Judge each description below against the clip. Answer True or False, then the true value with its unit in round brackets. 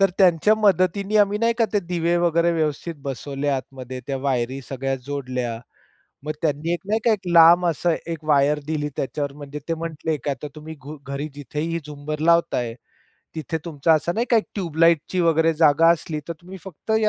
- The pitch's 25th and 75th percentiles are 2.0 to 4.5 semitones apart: True (3.3 semitones)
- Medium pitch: True (160 Hz)